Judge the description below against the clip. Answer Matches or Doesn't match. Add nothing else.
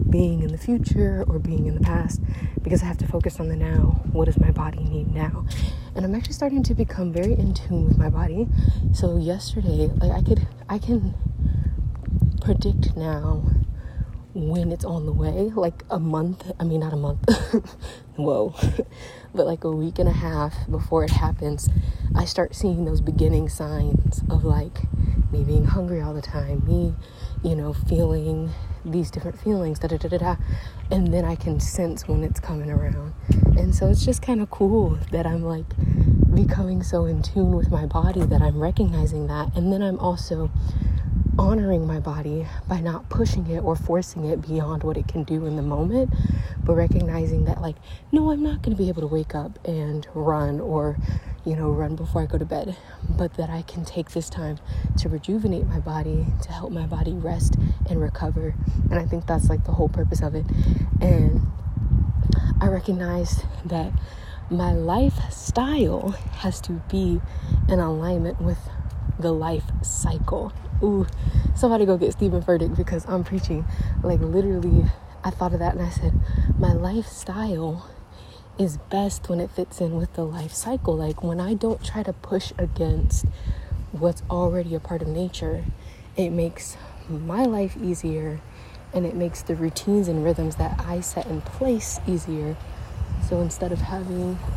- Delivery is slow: Doesn't match